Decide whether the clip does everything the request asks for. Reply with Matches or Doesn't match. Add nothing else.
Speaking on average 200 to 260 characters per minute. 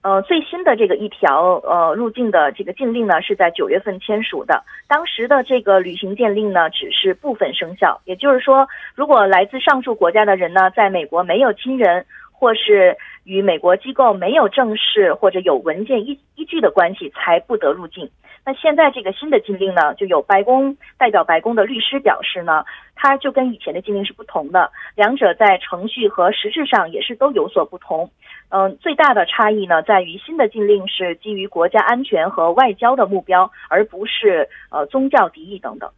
Doesn't match